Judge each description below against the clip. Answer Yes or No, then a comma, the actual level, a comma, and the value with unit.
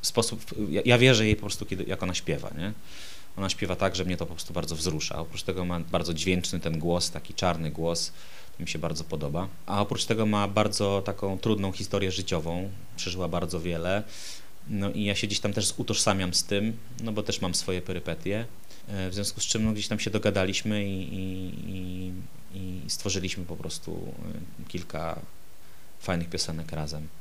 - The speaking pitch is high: No, very low, 95 Hz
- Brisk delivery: Yes, fast, 185 wpm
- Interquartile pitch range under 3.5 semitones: Yes, average, 2.9 semitones